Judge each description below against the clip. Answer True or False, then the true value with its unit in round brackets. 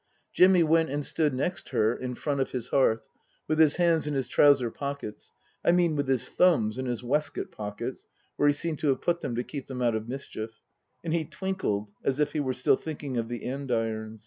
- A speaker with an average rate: False (220 wpm)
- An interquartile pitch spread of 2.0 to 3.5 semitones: False (4.5 semitones)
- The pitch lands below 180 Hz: True (135 Hz)